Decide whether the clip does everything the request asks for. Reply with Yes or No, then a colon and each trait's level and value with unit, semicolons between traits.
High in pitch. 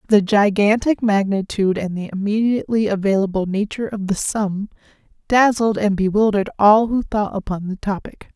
Yes: high, 205 Hz